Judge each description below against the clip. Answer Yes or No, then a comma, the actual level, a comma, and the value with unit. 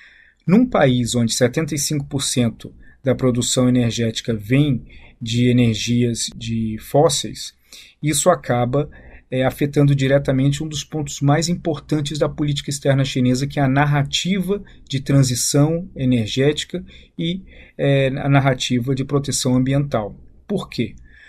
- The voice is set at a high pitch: No, medium, 140 Hz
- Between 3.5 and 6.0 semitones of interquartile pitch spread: No, average, 3.1 semitones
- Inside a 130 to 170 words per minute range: No, slow, 120 wpm